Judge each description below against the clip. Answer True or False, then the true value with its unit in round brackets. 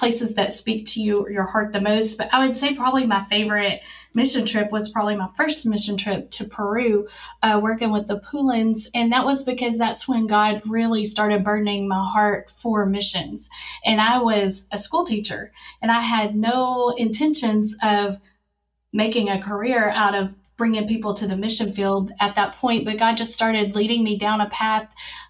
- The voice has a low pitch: False (215 Hz)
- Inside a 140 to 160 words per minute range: False (190 wpm)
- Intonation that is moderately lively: False (2.0 semitones)